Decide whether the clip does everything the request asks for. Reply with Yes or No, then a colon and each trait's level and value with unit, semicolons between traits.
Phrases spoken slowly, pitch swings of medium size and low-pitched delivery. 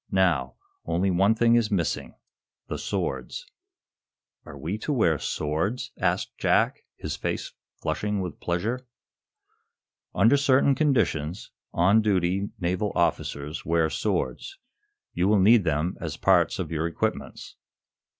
Yes: slow, 125 wpm; average, 4.7 semitones; very low, 95 Hz